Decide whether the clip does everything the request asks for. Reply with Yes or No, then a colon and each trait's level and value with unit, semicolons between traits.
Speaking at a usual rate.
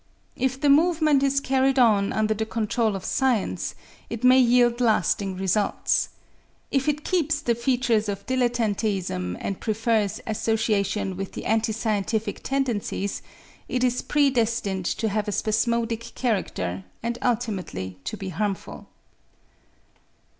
No: slow, 130 wpm